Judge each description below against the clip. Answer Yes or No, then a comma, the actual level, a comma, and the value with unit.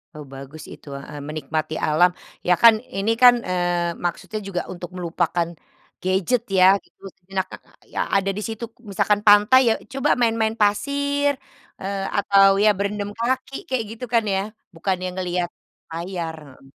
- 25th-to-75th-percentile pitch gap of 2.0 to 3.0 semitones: No, average, 4.2 semitones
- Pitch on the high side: Yes, high, 195 Hz